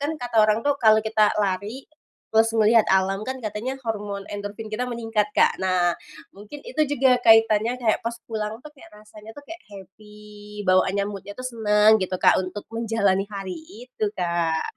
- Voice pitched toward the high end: Yes, high, 215 Hz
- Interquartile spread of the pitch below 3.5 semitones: Yes, narrow, 2.4 semitones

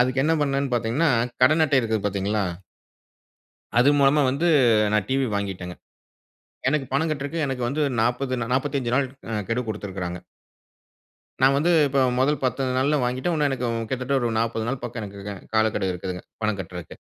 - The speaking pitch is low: Yes, low, 125 Hz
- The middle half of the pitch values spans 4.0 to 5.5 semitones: Yes, average, 4.4 semitones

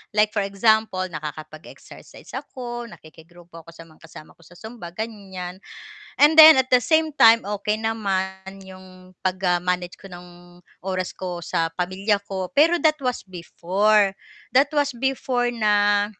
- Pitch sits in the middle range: No, high, 195 Hz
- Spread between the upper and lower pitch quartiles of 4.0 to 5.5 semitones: Yes, average, 4.4 semitones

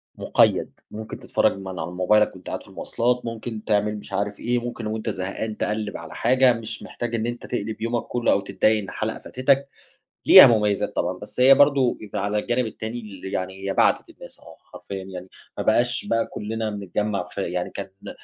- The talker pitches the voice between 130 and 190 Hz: No, low, 110 Hz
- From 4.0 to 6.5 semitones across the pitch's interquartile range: No, average, 3.3 semitones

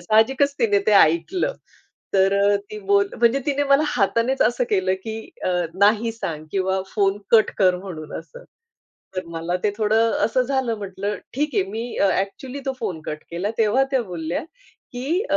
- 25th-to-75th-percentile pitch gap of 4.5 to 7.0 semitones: Yes, average, 4.8 semitones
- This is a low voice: No, high, 210 Hz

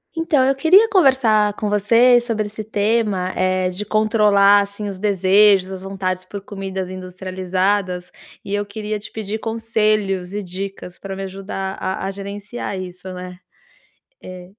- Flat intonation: Yes, narrow, 2.3 semitones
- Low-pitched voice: No, high, 200 Hz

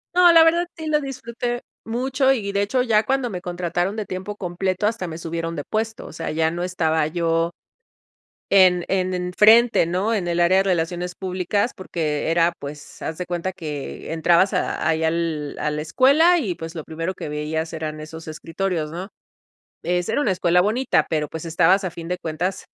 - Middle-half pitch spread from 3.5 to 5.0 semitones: Yes, average, 4.3 semitones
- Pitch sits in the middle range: Yes, medium, 180 Hz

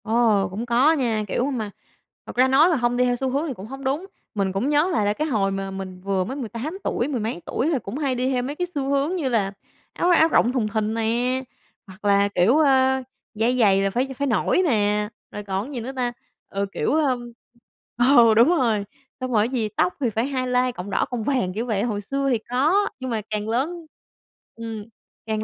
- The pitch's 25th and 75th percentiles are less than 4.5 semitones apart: Yes, average, 4.1 semitones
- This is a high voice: Yes, high, 240 Hz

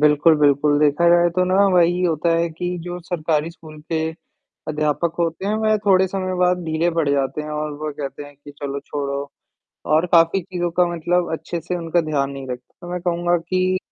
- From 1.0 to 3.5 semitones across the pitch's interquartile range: Yes, average, 2.9 semitones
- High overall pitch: No, medium, 165 Hz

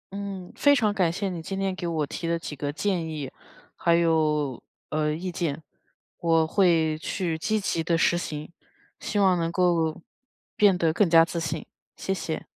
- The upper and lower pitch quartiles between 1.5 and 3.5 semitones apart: Yes, average, 2.8 semitones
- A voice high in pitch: No, medium, 170 Hz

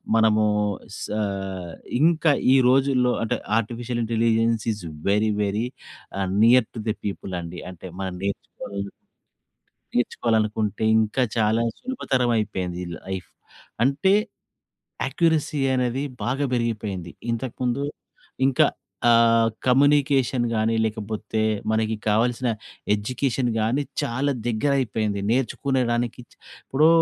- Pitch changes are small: No, average, 3.2 semitones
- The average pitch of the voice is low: Yes, low, 115 Hz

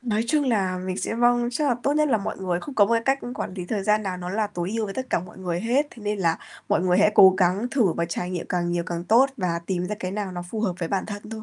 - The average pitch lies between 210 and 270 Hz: No, high, 200 Hz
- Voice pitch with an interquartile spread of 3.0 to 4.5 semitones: Yes, average, 4.1 semitones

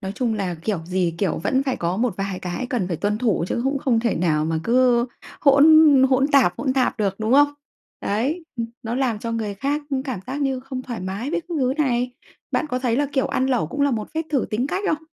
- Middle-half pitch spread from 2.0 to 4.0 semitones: No, average, 4.9 semitones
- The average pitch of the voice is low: No, high, 245 Hz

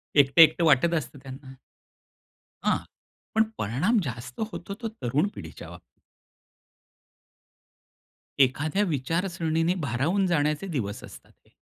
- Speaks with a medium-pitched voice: Yes, medium, 150 Hz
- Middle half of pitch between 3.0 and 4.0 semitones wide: No, average, 4.8 semitones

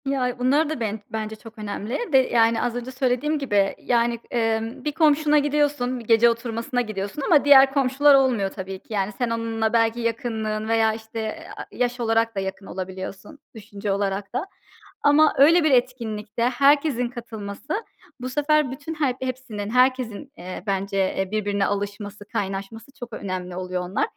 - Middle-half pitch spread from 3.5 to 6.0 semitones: Yes, average, 4.2 semitones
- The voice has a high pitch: Yes, high, 230 Hz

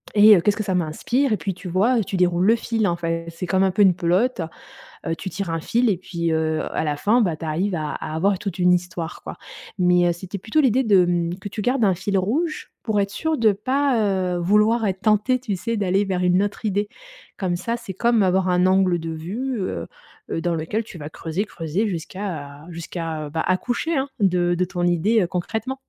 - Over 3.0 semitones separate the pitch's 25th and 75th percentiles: Yes, average, 3.7 semitones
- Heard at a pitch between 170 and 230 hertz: Yes, high, 190 Hz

